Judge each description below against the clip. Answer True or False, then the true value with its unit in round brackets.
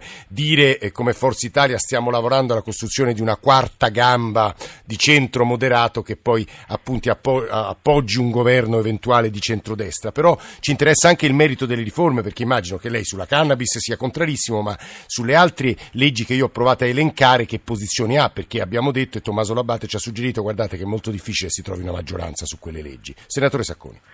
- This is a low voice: True (120 Hz)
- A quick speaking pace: True (185 wpm)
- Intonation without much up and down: False (3.4 semitones)